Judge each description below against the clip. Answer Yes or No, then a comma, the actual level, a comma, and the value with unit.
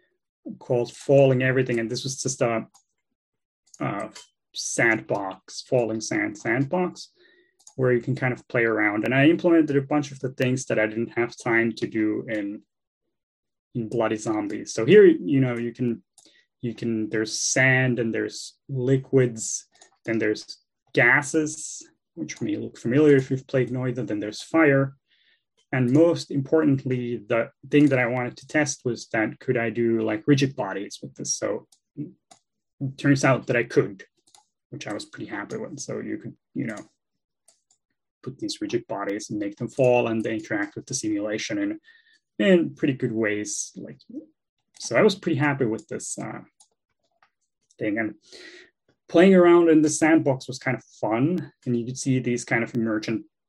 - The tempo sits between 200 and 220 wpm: No, average, 170 wpm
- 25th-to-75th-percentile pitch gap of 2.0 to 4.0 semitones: No, average, 5.1 semitones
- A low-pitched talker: Yes, low, 130 Hz